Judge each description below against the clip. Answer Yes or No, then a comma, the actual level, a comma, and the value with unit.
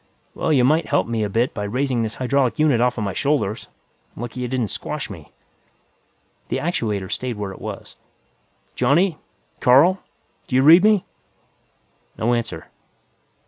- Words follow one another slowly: No, average, 150 wpm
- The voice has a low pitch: Yes, low, 125 Hz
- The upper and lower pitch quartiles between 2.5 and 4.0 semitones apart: No, average, 4.4 semitones